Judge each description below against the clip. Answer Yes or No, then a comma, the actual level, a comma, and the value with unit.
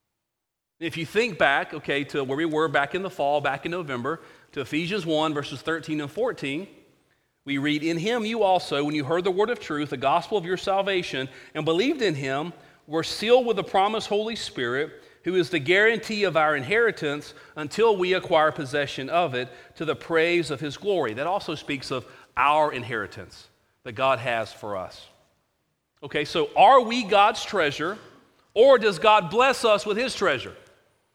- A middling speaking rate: Yes, average, 185 wpm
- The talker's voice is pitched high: No, medium, 165 Hz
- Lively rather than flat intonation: Yes, wide, 6.1 semitones